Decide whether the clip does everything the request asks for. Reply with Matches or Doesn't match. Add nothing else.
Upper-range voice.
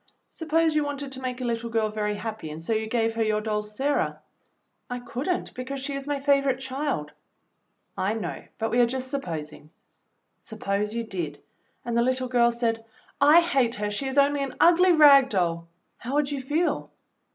Matches